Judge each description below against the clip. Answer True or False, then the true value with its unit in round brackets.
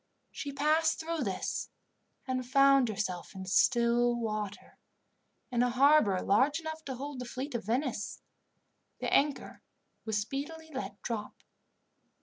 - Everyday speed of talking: False (130 wpm)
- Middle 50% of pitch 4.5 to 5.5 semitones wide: True (4.8 semitones)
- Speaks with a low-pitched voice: False (250 Hz)